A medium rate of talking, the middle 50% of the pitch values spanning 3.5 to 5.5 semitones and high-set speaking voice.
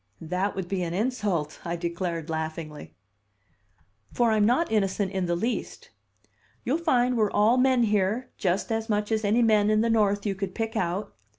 Yes: average, 180 wpm; average, 3.9 semitones; high, 205 Hz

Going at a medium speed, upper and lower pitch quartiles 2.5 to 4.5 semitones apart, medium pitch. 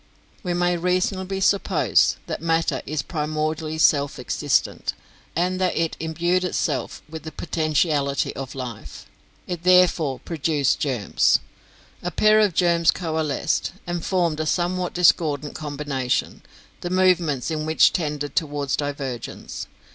No: slow, 125 wpm; average, 3.3 semitones; medium, 160 Hz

